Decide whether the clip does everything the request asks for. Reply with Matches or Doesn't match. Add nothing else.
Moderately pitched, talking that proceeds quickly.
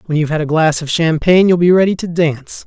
Matches